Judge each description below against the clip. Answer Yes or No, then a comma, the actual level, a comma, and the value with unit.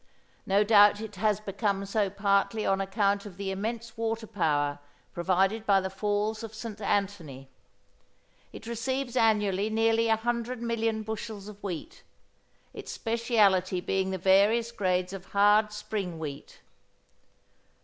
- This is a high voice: Yes, high, 205 Hz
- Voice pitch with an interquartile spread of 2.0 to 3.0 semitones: Yes, narrow, 2.6 semitones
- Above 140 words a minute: No, slow, 135 wpm